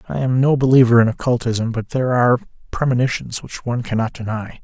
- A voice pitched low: Yes, low, 120 Hz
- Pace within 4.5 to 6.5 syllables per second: Yes, 6.3 syllables/s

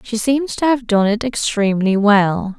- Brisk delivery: No, average, 185 wpm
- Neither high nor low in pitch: No, high, 220 Hz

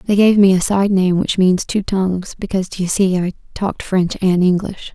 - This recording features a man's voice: No, female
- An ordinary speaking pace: No, fast, 220 wpm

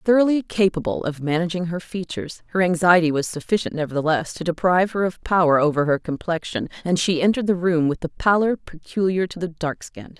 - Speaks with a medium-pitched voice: Yes, medium, 175 Hz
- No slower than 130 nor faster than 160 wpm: No, average, 190 wpm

